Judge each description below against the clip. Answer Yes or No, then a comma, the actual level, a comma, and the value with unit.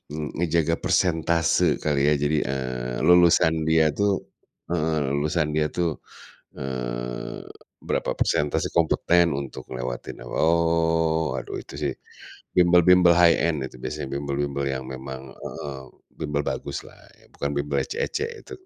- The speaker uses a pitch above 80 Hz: No, very low, 75 Hz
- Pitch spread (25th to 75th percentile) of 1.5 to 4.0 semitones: Yes, average, 3.4 semitones